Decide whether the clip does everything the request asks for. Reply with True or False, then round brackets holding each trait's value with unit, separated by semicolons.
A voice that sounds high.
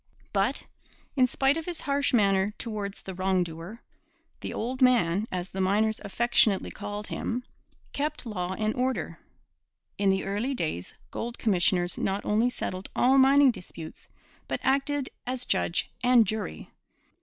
True (215 Hz)